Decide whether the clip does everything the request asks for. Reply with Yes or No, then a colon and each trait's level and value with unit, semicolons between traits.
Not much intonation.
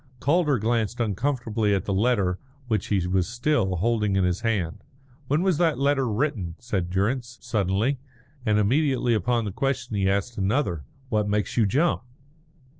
No: average, 4.8 semitones